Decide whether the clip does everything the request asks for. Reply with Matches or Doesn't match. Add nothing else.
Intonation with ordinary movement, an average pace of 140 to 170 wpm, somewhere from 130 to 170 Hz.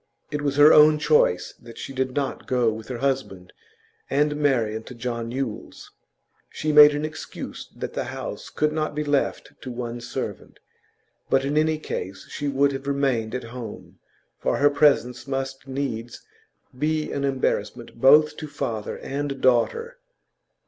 Matches